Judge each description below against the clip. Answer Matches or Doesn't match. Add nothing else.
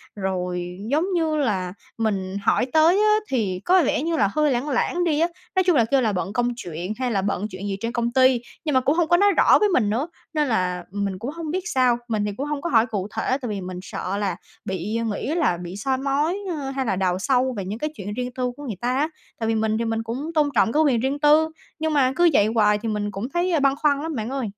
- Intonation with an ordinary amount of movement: Doesn't match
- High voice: Matches